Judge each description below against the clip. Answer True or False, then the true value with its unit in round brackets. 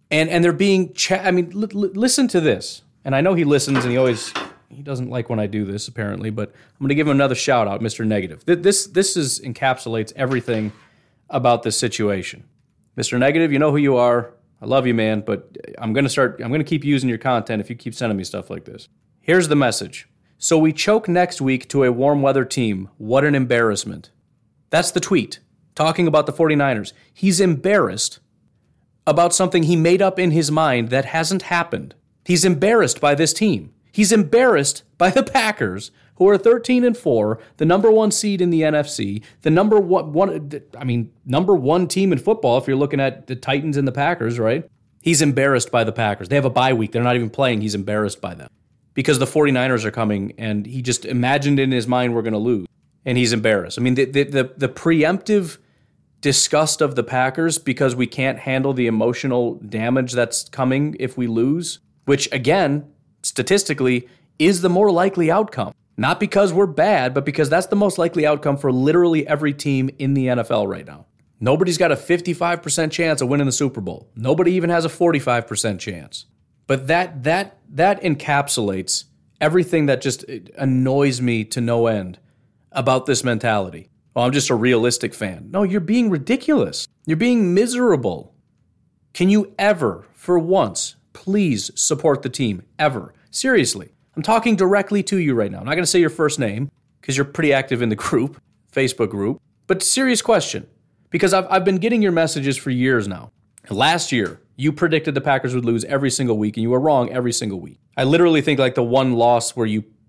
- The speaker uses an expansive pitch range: True (6.1 semitones)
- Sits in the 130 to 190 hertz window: True (140 Hz)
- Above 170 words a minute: True (200 wpm)